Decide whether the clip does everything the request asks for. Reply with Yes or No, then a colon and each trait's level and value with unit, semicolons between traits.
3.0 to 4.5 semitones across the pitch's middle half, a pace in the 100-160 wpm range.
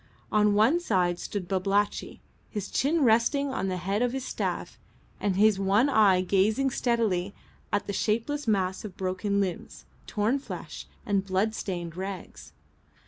Yes: average, 3.3 semitones; average, 145 wpm